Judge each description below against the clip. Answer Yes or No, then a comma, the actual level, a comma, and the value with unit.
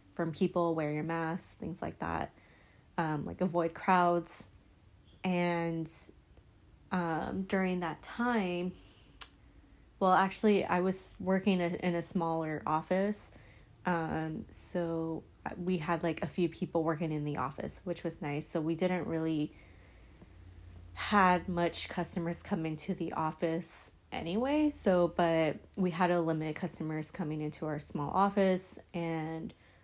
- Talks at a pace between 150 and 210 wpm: No, slow, 135 wpm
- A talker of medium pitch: Yes, medium, 165 Hz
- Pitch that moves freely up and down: No, average, 2.9 semitones